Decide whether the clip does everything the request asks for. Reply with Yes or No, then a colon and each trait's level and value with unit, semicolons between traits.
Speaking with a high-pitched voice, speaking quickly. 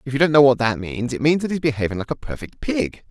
No: low, 135 Hz; fast, 310 wpm